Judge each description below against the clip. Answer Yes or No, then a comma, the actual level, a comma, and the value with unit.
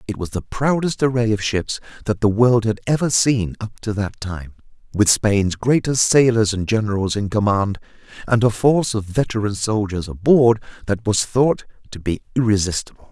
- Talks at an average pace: Yes, average, 175 wpm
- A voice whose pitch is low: Yes, low, 110 Hz